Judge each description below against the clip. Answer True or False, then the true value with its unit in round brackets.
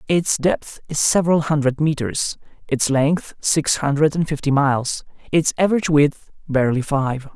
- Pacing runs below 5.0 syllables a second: True (4.8 syllables/s)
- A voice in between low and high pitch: True (150 Hz)